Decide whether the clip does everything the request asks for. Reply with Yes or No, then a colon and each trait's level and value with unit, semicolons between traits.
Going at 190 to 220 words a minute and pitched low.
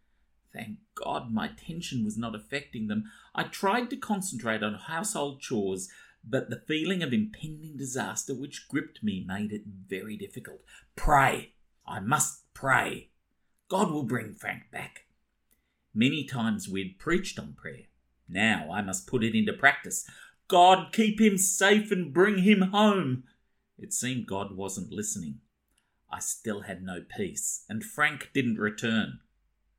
No: average, 145 wpm; low, 130 Hz